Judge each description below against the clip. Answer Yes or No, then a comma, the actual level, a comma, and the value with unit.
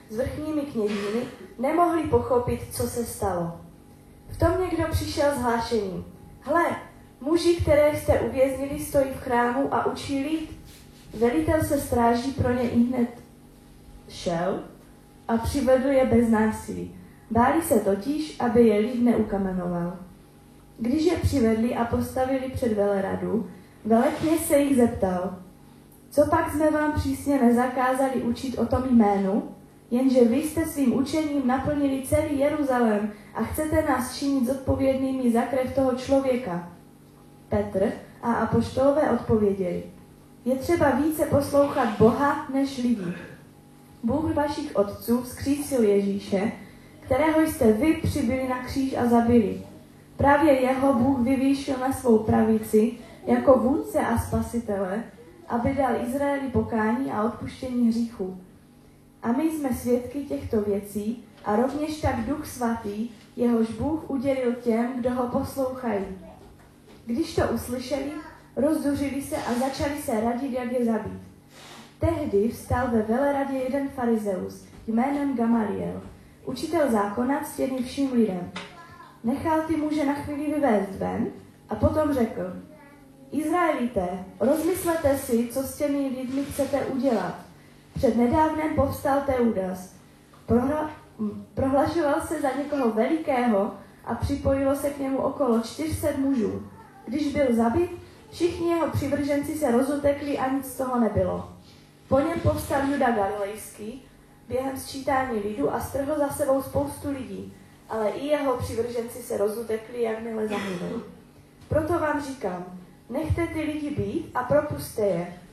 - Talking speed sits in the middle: Yes, average, 130 wpm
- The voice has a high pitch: Yes, very high, 255 Hz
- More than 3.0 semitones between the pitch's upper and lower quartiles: Yes, average, 4.4 semitones